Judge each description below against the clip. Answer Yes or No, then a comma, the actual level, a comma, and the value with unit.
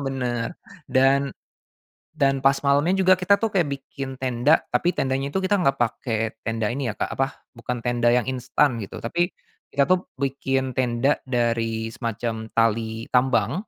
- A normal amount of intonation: Yes, average, 3.1 semitones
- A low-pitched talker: Yes, low, 130 Hz